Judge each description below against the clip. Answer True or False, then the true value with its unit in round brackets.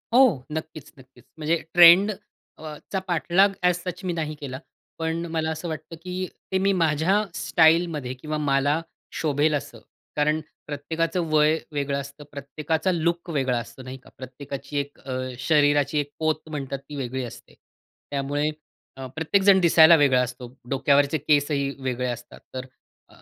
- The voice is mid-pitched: True (150 Hz)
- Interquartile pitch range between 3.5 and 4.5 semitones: False (3.1 semitones)